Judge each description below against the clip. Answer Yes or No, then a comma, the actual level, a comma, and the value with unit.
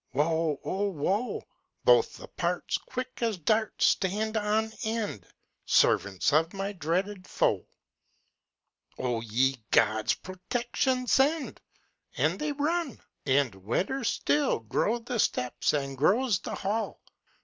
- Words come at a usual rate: No, slow, 120 wpm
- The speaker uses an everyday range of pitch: No, wide, 8.5 semitones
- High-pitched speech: Yes, high, 195 Hz